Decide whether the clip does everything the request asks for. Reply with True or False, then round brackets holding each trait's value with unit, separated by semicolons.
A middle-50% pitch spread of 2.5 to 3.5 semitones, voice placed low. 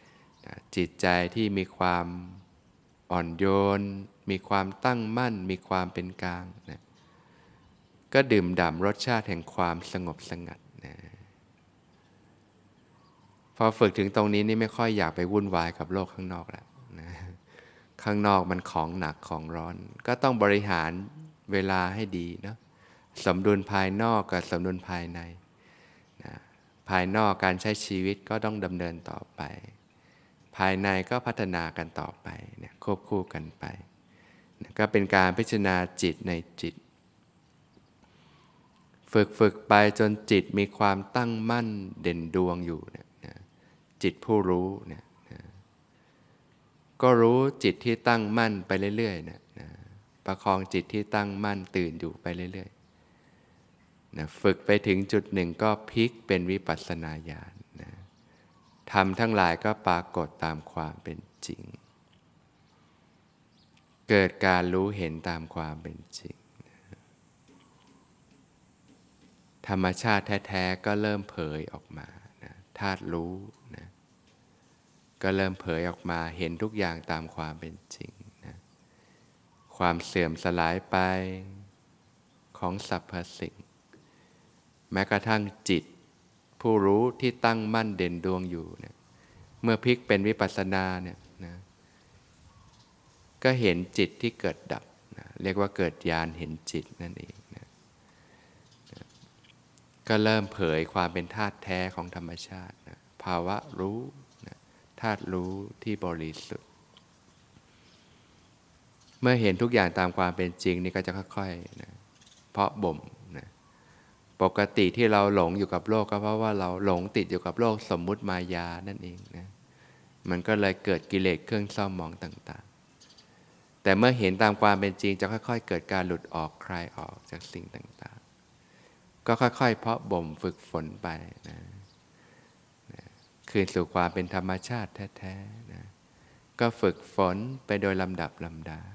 True (3.2 semitones; 95 Hz)